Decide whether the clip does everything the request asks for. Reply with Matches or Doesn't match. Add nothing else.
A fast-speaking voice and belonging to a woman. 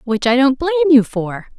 Matches